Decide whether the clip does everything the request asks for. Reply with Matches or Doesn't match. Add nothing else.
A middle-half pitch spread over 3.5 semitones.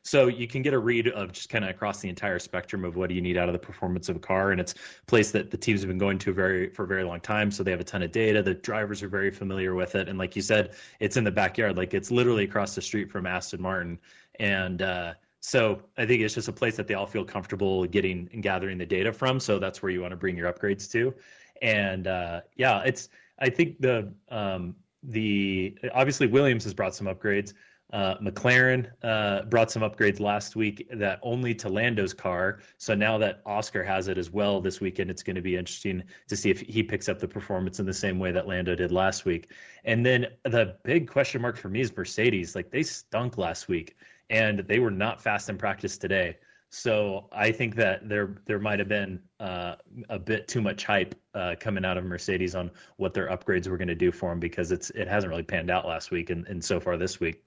Doesn't match